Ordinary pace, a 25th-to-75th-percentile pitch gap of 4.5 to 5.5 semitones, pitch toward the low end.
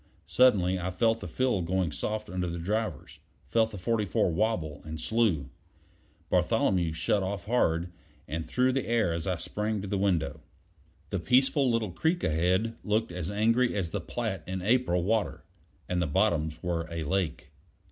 Yes: average, 165 wpm; average, 4.9 semitones; very low, 95 Hz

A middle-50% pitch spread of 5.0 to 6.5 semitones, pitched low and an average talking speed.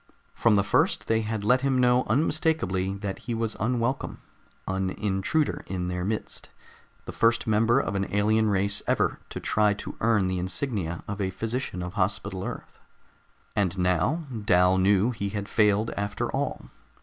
No: average, 3.3 semitones; low, 105 Hz; average, 165 wpm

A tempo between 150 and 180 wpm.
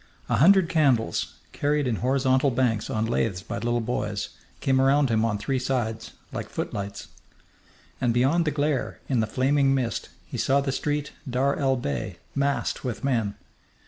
Yes: average, 165 wpm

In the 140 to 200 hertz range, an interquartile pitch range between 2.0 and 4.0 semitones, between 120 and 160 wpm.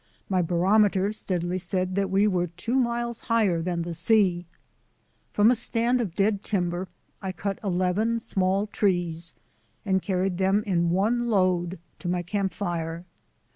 Yes: high, 190 Hz; average, 3.1 semitones; average, 150 wpm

